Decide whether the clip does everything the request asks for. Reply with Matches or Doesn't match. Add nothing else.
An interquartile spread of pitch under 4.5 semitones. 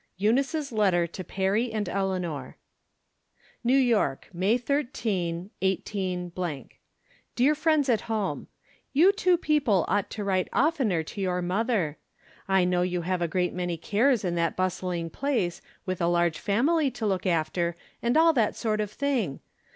Doesn't match